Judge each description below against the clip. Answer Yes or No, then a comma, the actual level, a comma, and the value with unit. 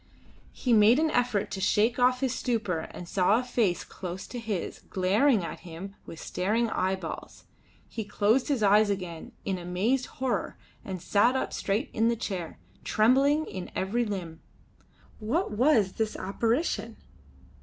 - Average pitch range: Yes, average, 4.6 semitones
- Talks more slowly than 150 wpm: No, average, 155 wpm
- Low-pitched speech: No, high, 215 Hz